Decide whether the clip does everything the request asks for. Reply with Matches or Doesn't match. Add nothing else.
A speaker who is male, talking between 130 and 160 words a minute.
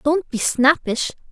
Doesn't match